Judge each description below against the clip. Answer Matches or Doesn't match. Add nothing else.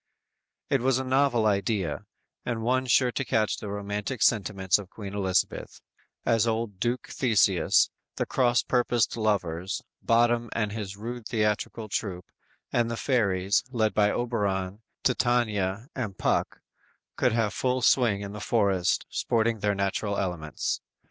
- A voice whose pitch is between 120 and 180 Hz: Doesn't match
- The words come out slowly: Doesn't match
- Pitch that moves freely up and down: Doesn't match